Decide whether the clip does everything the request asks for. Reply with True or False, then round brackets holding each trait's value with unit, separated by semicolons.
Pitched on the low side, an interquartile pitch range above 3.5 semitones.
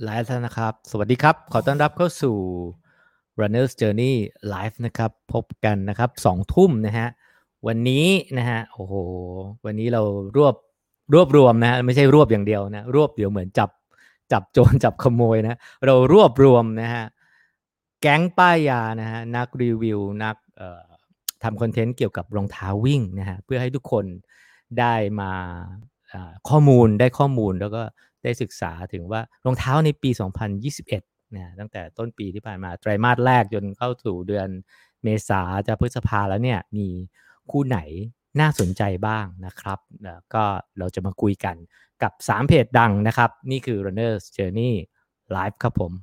True (110 Hz; 3.9 semitones)